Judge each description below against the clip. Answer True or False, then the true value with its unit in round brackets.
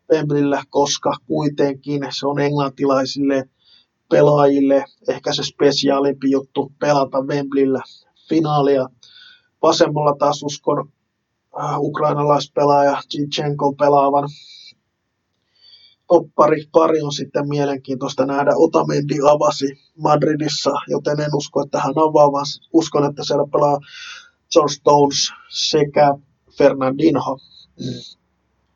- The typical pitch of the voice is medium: True (145 Hz)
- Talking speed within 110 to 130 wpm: False (95 wpm)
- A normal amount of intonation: False (1.3 semitones)